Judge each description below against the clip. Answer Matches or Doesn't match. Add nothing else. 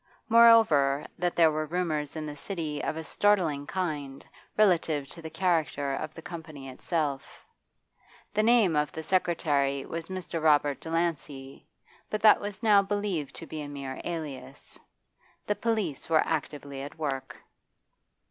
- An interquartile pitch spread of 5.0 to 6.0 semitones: Doesn't match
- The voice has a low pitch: Doesn't match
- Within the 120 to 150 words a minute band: Matches